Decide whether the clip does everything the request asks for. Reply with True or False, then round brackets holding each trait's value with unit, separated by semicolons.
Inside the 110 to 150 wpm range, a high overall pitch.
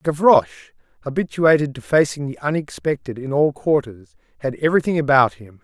False (140 wpm; 140 Hz)